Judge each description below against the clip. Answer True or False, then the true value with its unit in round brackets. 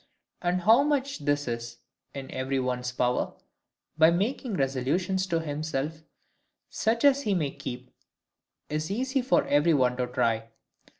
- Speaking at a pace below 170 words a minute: True (140 wpm)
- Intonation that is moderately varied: False (7.2 semitones)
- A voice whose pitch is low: False (150 Hz)